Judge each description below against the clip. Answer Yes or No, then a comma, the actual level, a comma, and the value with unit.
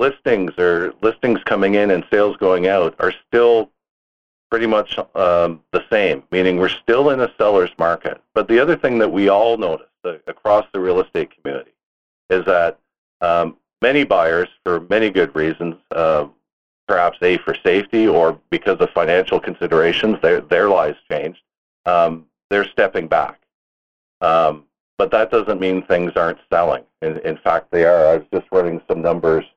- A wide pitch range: Yes, wide, 6.3 semitones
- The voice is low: Yes, low, 100 Hz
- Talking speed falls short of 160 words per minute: No, average, 165 wpm